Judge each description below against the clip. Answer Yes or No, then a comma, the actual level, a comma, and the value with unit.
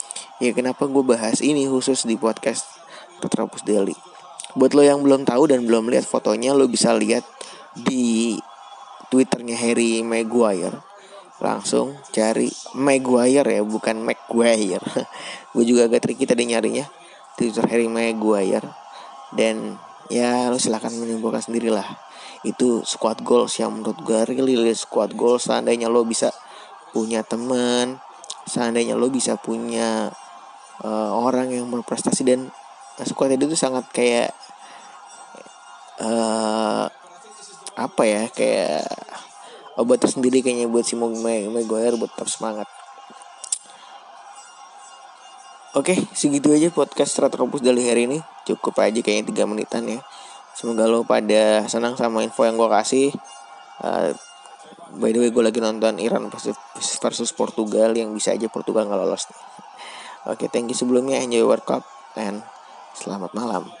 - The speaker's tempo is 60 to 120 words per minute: No, average, 130 wpm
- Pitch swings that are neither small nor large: No, narrow, 1.9 semitones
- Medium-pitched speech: No, low, 115 Hz